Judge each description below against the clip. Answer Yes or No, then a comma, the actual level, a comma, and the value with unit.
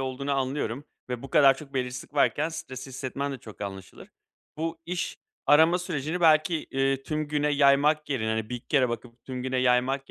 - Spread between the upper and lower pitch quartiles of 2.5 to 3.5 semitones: Yes, average, 2.9 semitones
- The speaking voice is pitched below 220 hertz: Yes, low, 135 Hz